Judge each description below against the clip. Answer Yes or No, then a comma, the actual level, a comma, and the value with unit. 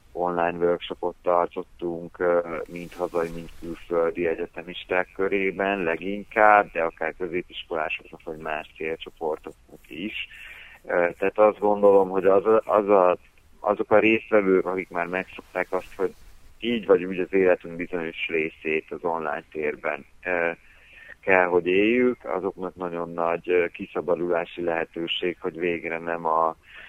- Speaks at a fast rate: No, average, 120 wpm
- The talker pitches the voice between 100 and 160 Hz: No, very low, 90 Hz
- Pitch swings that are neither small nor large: No, narrow, 2.3 semitones